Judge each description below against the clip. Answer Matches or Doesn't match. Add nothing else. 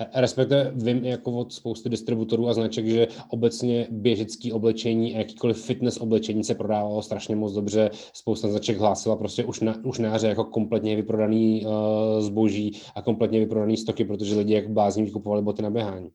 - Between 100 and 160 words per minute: Doesn't match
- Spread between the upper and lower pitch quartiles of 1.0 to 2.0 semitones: Matches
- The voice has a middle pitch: Doesn't match